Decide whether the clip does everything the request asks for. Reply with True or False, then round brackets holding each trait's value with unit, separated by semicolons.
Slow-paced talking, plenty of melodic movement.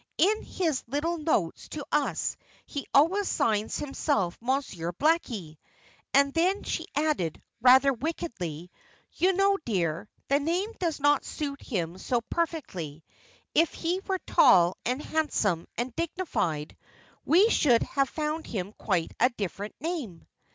True (130 wpm; 9.0 semitones)